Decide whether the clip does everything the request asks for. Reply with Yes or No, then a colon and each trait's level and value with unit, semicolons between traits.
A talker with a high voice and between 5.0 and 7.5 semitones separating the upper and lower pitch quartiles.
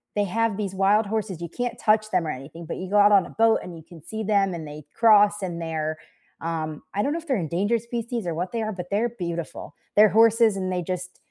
No: high, 195 Hz; average, 4.3 semitones